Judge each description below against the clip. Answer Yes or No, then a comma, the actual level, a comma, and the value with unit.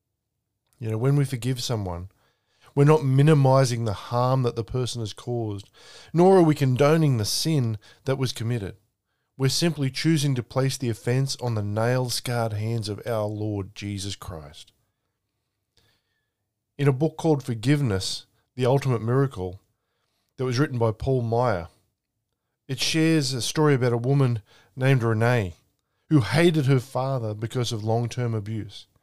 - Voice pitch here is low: Yes, low, 120 Hz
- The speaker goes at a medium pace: Yes, average, 155 wpm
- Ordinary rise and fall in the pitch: Yes, average, 3.4 semitones